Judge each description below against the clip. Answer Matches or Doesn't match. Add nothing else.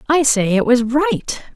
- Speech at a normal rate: Matches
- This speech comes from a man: Doesn't match